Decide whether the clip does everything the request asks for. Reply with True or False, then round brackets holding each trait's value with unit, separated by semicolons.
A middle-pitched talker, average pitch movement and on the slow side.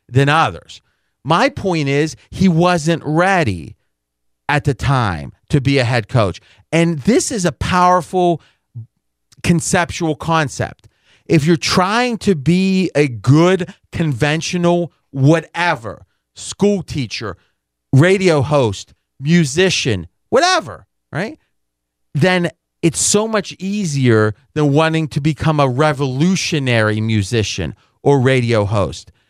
False (150 Hz; 7.0 semitones; 110 wpm)